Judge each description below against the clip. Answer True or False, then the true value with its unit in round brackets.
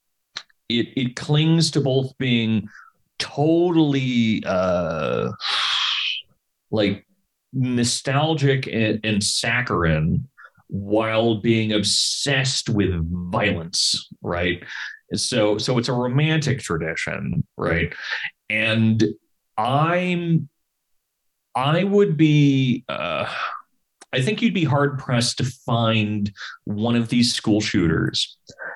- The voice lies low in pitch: True (120 Hz)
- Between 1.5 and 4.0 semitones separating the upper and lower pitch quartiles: False (5.0 semitones)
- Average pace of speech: False (90 wpm)